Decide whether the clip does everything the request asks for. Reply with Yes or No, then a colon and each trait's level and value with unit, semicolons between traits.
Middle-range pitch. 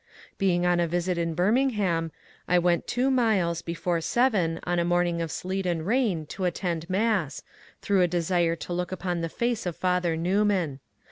Yes: medium, 175 Hz